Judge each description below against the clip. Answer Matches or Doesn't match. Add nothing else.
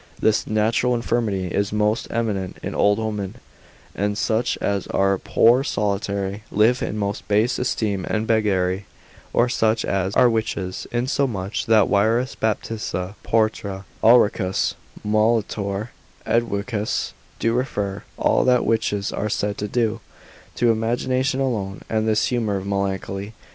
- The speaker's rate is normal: Doesn't match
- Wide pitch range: Doesn't match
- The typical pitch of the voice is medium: Doesn't match